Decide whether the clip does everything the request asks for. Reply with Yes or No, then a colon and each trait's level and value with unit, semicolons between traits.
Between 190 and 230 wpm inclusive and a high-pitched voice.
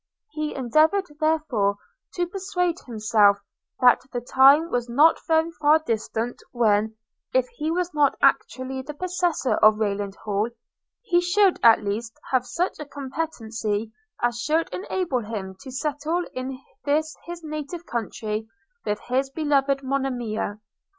No: slow, 135 wpm; very high, 270 Hz